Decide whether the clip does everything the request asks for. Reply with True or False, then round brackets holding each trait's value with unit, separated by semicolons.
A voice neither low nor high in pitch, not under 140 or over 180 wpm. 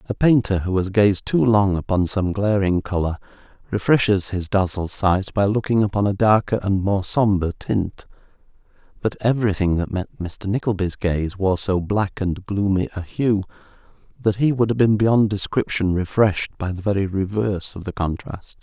False (100 Hz; 170 wpm)